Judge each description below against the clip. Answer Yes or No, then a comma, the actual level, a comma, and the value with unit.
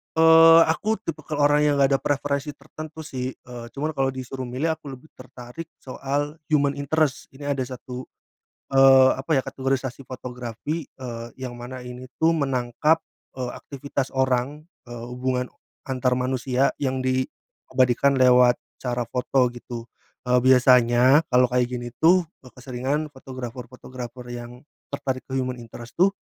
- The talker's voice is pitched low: Yes, low, 130 Hz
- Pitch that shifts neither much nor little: No, narrow, 2.2 semitones